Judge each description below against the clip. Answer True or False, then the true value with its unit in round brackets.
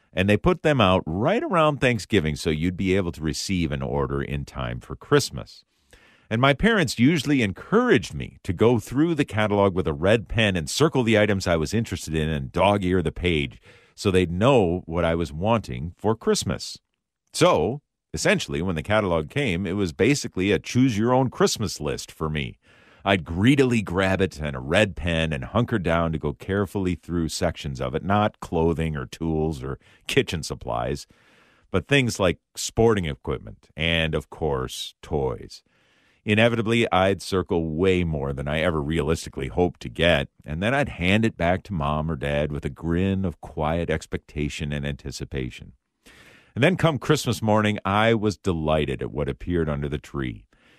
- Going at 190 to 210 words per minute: False (180 wpm)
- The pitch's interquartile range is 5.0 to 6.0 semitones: True (5.6 semitones)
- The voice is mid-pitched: False (90 Hz)